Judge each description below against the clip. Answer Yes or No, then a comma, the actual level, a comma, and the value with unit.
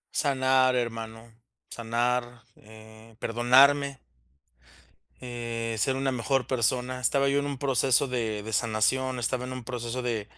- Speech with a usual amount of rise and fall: No, narrow, 2.3 semitones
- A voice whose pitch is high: No, low, 125 Hz